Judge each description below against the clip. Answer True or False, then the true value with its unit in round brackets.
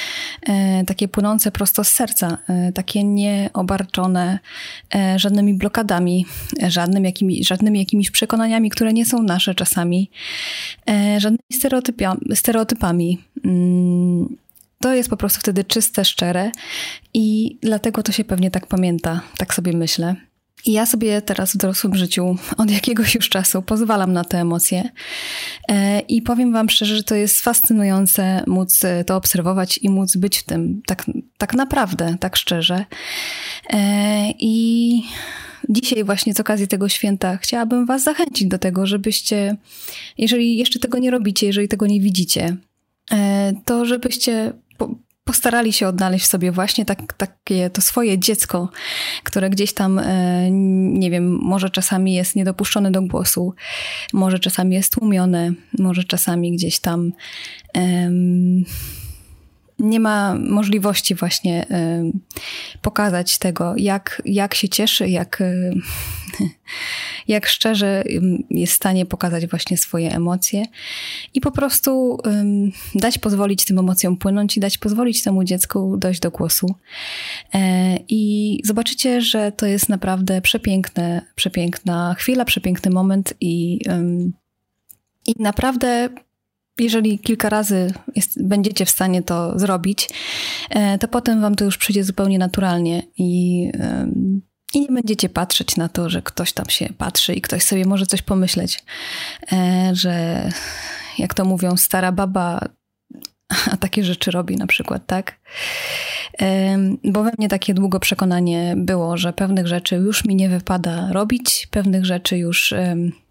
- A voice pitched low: False (195 Hz)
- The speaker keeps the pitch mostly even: False (3.4 semitones)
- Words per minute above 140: False (130 wpm)